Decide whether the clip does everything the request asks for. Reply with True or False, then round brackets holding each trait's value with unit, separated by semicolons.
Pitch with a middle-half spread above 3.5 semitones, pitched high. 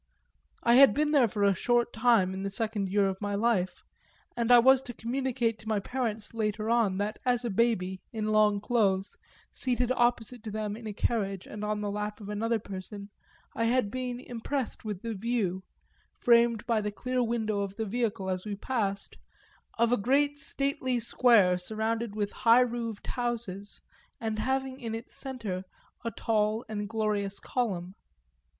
False (2.8 semitones; 225 Hz)